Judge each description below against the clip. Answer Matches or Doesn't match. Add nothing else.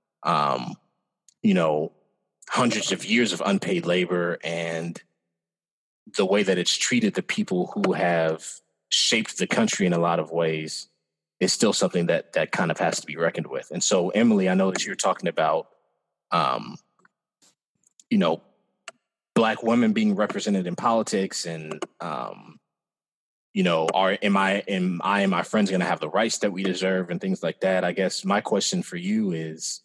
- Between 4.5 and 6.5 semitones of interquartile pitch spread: Matches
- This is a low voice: Matches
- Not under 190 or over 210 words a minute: Doesn't match